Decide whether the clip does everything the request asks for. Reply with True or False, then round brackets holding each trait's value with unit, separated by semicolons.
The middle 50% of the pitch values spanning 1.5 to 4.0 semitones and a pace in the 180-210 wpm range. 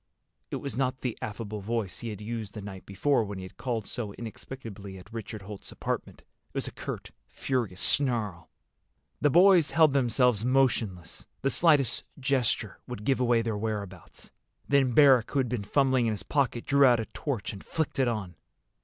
False (4.4 semitones; 185 wpm)